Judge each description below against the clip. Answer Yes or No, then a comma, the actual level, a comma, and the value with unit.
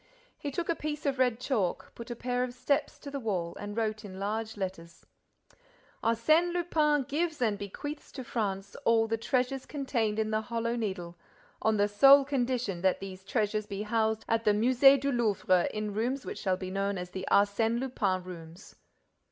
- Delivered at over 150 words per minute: Yes, average, 185 wpm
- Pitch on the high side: Yes, high, 225 Hz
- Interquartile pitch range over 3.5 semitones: Yes, average, 4.4 semitones